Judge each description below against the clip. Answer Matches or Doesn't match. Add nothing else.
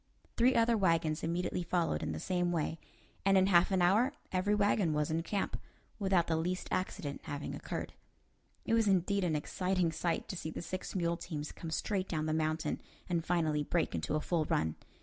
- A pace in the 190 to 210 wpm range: Matches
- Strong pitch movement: Doesn't match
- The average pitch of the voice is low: Doesn't match